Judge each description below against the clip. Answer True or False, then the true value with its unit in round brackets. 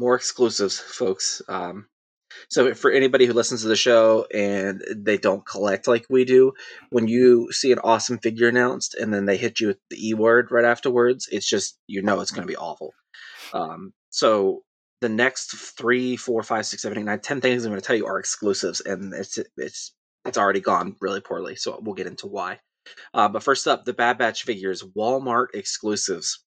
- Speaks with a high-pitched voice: False (120 Hz)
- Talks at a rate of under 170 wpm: False (200 wpm)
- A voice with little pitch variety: True (2.2 semitones)